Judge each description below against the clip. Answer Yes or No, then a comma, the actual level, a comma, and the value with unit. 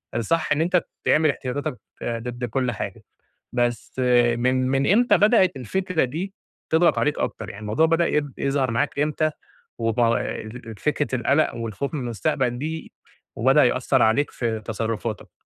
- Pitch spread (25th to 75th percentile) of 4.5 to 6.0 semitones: Yes, average, 4.8 semitones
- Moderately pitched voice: No, low, 130 Hz